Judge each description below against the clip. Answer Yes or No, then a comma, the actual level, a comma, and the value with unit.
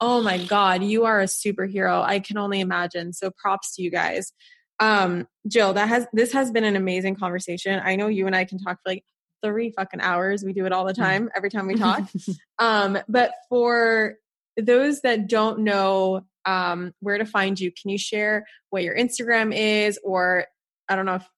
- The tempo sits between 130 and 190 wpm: No, average, 200 wpm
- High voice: Yes, high, 195 Hz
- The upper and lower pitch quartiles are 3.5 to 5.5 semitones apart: No, narrow, 2.6 semitones